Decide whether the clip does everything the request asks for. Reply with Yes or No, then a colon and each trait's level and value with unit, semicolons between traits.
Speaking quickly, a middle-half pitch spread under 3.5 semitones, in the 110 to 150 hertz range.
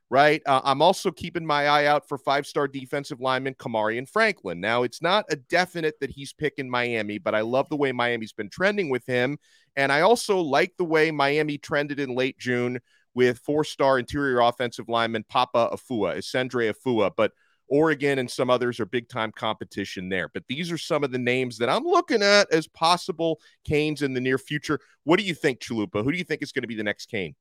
No: fast, 210 wpm; average, 3.9 semitones; medium, 140 Hz